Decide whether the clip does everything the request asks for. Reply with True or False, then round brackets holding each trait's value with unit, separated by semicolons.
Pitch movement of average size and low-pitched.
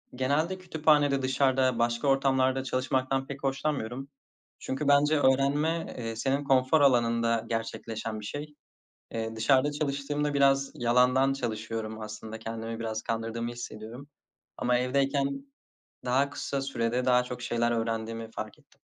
True (3.3 semitones; 130 Hz)